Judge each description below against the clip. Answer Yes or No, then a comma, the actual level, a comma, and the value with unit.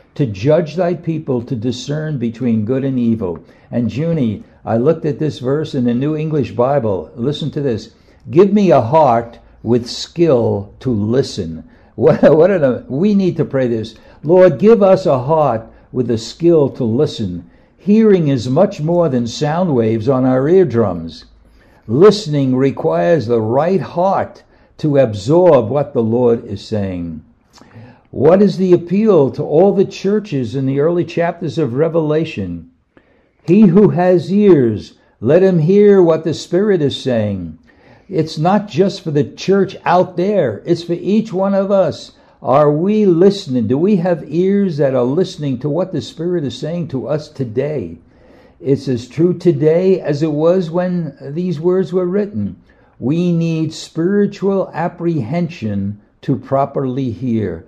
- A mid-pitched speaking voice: Yes, medium, 150 Hz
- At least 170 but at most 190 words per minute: No, average, 160 wpm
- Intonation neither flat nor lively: No, wide, 6.6 semitones